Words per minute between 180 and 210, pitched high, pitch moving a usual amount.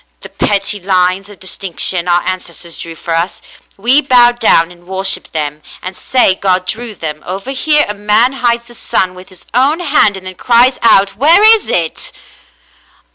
Yes: average, 185 wpm; high, 195 Hz; average, 4.8 semitones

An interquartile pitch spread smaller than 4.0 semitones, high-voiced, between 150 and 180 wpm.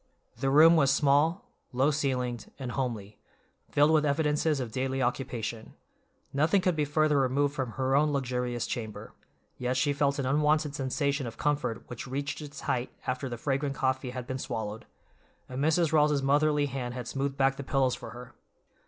No: average, 2.8 semitones; low, 135 Hz; average, 175 wpm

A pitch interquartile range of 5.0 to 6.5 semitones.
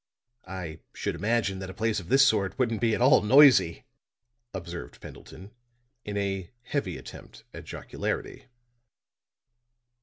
No: average, 4.0 semitones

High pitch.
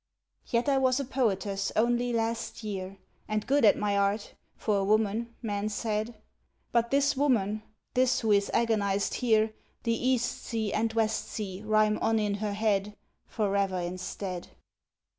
Yes: high, 215 Hz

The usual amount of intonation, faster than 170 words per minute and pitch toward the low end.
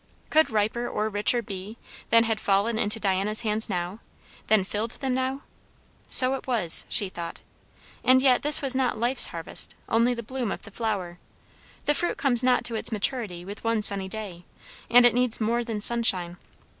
No: average, 3.4 semitones; average, 180 wpm; high, 225 Hz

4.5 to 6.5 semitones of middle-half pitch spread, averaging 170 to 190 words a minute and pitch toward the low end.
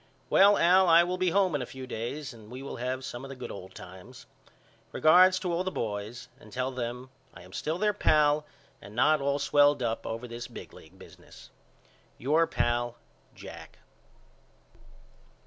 Yes: wide, 5.6 semitones; average, 180 wpm; low, 130 Hz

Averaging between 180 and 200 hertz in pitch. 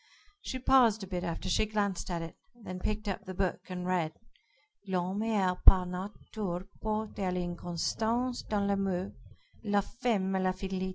Yes: high, 190 Hz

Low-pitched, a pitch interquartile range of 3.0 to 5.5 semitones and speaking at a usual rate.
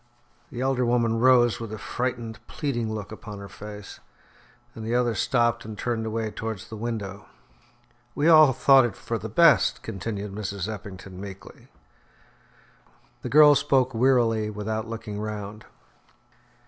No: low, 110 Hz; narrow, 2.6 semitones; average, 145 wpm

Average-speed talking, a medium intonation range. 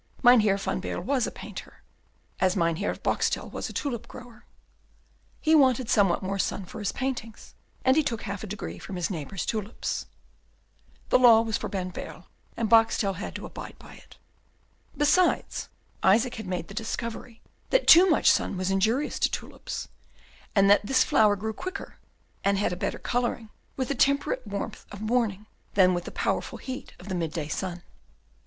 Yes: average, 175 wpm; average, 4.2 semitones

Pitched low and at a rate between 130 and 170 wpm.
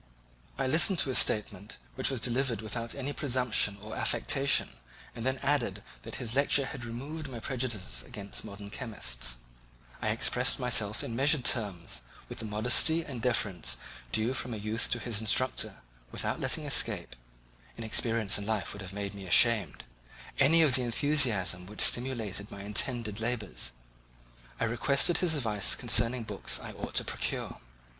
Yes: low, 115 Hz; average, 160 wpm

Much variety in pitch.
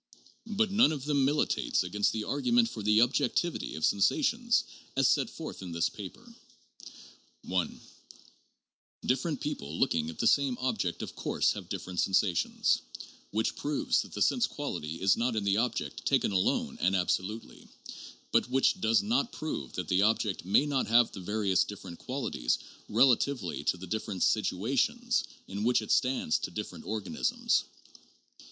Yes: wide, 6.8 semitones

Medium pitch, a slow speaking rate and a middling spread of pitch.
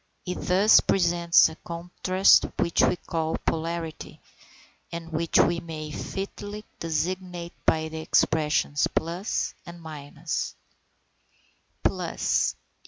No: medium, 170 Hz; slow, 105 wpm; narrow, 2.0 semitones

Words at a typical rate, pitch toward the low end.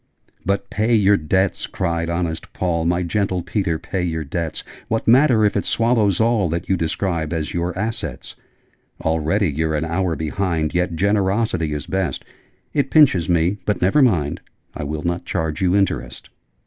Yes: average, 165 wpm; very low, 90 Hz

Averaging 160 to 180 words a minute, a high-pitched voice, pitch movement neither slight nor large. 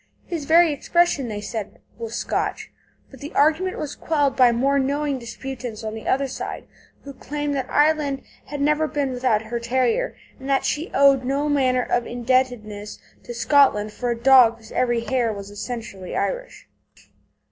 Yes: average, 170 wpm; very high, 260 Hz; average, 3.6 semitones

